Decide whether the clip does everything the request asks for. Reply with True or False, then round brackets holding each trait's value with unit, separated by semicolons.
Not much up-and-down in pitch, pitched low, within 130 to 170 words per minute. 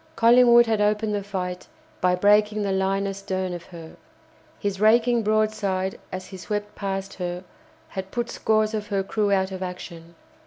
False (2.3 semitones; 195 Hz; 165 wpm)